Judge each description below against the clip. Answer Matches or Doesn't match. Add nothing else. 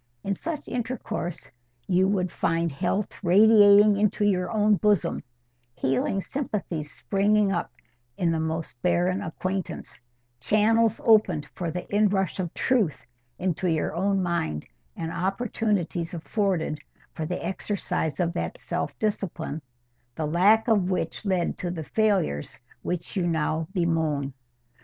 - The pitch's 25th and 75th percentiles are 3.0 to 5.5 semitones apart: Matches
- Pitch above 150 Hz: Matches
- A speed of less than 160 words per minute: Matches